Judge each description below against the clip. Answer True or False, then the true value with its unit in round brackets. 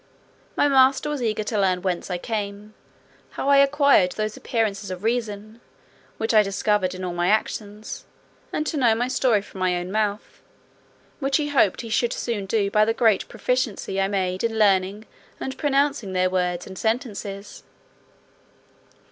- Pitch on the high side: True (215 Hz)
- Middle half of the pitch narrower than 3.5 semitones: False (3.8 semitones)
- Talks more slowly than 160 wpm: False (165 wpm)